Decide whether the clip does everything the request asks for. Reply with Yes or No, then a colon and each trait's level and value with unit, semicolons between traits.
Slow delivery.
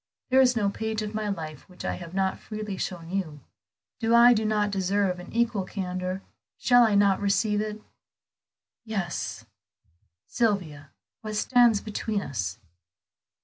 No: average, 145 wpm